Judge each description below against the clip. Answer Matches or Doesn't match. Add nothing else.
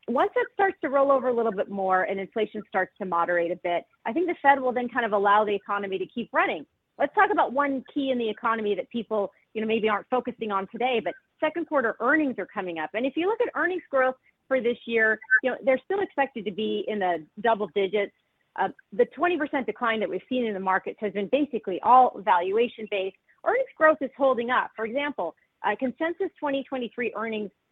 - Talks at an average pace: Doesn't match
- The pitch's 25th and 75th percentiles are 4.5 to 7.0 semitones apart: Matches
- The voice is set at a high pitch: Matches